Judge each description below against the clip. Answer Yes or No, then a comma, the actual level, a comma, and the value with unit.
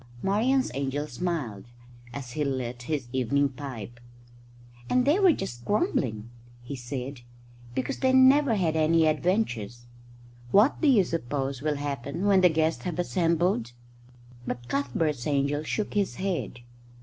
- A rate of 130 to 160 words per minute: Yes, slow, 135 wpm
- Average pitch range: No, wide, 6.7 semitones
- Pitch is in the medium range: Yes, medium, 150 Hz